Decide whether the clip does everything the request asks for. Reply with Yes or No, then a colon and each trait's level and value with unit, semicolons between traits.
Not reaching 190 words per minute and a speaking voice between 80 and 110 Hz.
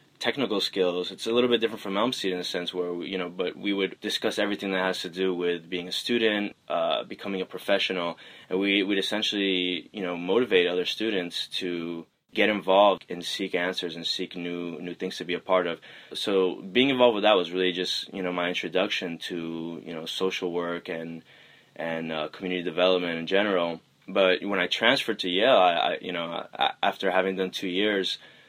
No: fast, 205 wpm; very low, 90 Hz